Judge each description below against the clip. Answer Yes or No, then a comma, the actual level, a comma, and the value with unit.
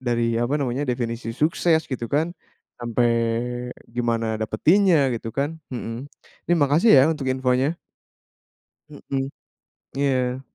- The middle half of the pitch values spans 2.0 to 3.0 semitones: No, average, 3.6 semitones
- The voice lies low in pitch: Yes, low, 130 Hz